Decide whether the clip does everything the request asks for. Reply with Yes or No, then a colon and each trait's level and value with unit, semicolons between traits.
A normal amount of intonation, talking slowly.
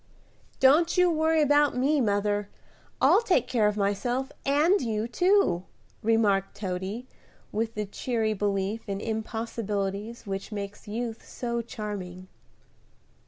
Yes: average, 4.2 semitones; slow, 120 wpm